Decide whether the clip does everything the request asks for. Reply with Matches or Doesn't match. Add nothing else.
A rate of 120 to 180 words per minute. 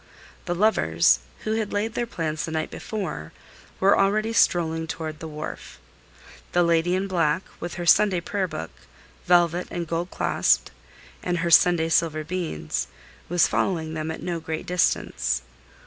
Matches